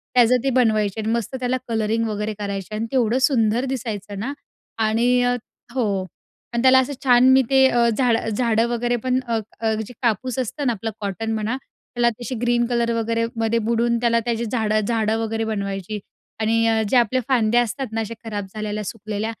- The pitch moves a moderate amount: No, narrow, 2.1 semitones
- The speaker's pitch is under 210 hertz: No, high, 230 Hz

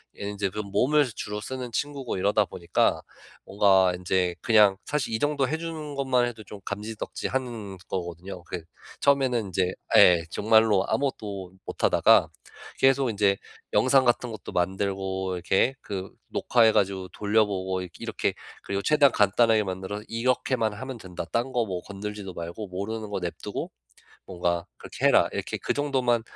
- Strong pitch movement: No, average, 4.4 semitones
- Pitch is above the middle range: No, low, 105 Hz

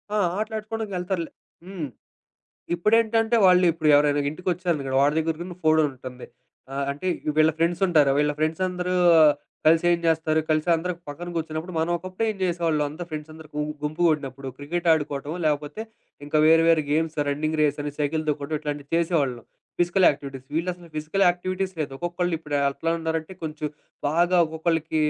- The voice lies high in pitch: No, medium, 160 Hz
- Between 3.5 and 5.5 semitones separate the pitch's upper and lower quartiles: No, average, 2.8 semitones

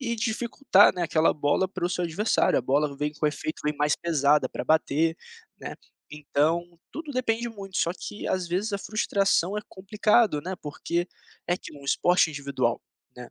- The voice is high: No, medium, 175 Hz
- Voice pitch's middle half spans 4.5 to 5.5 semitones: Yes, average, 5.2 semitones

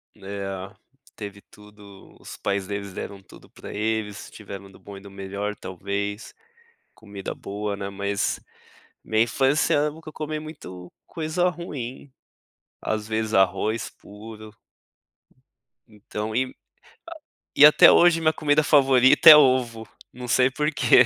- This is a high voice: No, low, 110 Hz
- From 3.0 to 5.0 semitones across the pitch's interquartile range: No, wide, 5.4 semitones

